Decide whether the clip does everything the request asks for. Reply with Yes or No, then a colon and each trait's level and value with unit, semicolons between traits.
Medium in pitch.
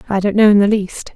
No: high, 205 Hz